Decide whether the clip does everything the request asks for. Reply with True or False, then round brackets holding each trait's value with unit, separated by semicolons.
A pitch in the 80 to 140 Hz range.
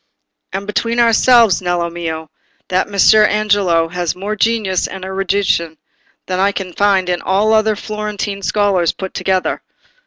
False (195 Hz)